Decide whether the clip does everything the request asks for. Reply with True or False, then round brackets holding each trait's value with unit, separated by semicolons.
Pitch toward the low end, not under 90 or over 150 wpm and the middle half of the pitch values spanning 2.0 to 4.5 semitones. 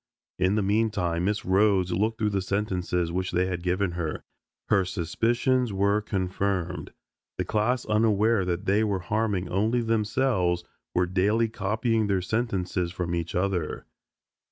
True (100 Hz; 145 wpm; 3.1 semitones)